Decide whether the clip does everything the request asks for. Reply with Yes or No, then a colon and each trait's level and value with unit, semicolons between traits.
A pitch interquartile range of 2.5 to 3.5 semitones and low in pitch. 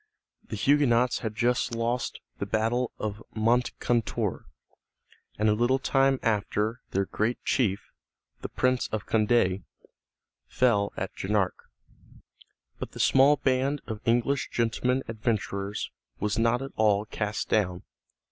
Yes: average, 3.1 semitones; low, 115 Hz